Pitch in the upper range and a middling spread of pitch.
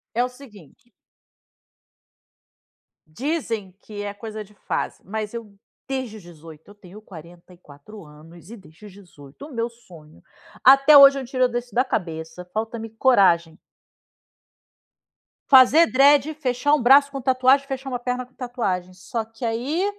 No: high, 225 Hz; wide, 6.0 semitones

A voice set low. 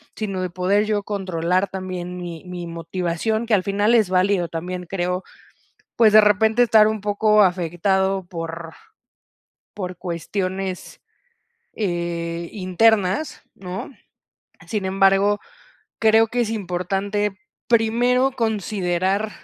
No: high, 195 Hz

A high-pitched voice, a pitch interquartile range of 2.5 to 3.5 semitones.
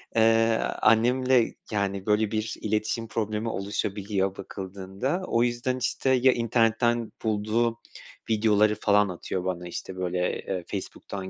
No: low, 110 Hz; average, 2.8 semitones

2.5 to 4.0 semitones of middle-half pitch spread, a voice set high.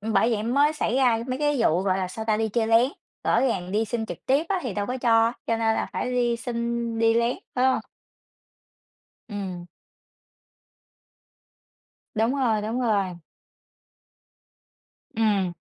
Yes: average, 2.8 semitones; high, 225 Hz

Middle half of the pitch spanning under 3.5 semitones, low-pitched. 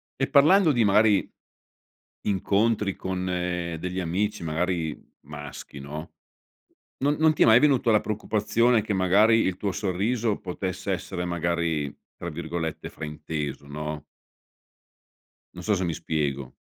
No: average, 4.8 semitones; very low, 90 Hz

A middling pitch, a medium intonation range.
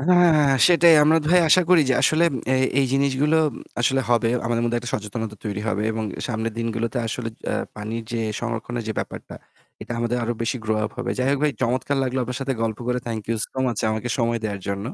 No: low, 120 Hz; average, 3.1 semitones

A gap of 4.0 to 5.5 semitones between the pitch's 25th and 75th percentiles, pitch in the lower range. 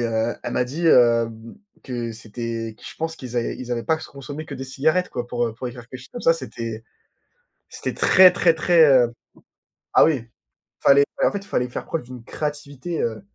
Yes: average, 5.0 semitones; low, 125 Hz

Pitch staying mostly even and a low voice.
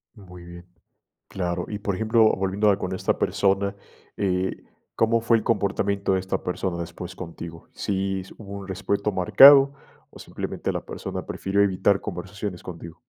Yes: narrow, 2.0 semitones; very low, 95 Hz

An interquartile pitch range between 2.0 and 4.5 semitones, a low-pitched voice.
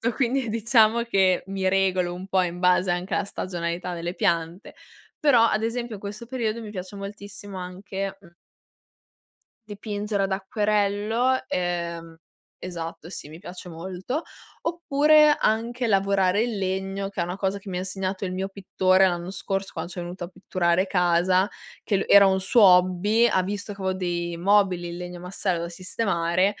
No: narrow, 2.6 semitones; high, 190 Hz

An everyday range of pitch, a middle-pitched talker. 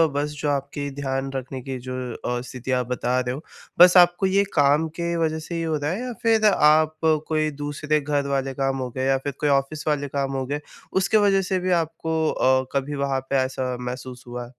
Yes: average, 3.1 semitones; medium, 145 Hz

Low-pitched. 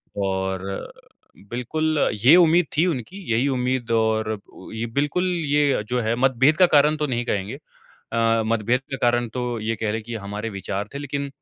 Yes: low, 120 Hz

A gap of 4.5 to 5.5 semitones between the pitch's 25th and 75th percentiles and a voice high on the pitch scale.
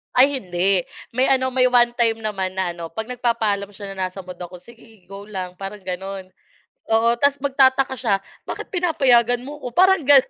Yes: average, 5.2 semitones; high, 225 Hz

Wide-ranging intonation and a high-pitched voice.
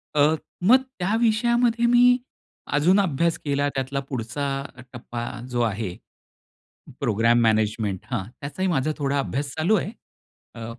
No: wide, 8.0 semitones; medium, 140 Hz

